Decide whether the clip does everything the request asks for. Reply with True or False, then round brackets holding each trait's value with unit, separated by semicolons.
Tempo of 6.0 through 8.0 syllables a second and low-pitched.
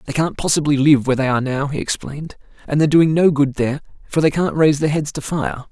False (6.6 syllables/s; 145 Hz)